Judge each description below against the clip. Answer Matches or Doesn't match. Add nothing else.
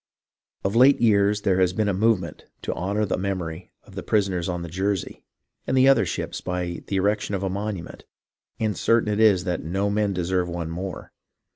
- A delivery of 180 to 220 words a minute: Matches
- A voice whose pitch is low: Matches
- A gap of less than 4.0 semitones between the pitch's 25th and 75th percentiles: Matches